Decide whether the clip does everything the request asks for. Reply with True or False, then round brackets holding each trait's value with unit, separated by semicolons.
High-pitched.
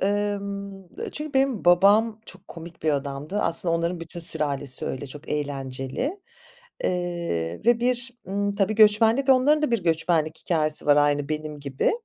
False (175 Hz)